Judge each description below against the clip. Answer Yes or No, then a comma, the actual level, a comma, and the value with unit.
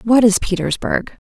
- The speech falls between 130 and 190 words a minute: Yes, average, 140 wpm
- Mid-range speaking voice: No, high, 215 Hz